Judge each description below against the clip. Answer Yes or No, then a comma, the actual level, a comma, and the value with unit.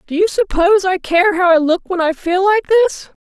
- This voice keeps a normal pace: No, fast, 240 wpm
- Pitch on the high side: Yes, very high, 355 Hz